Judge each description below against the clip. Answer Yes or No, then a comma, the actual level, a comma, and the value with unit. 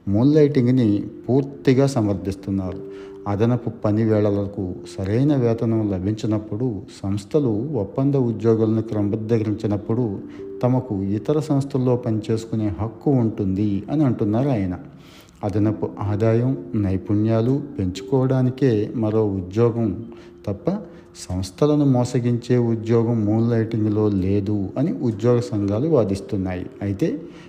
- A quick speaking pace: No, average, 85 wpm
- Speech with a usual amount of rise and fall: Yes, average, 3.2 semitones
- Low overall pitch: Yes, low, 110 Hz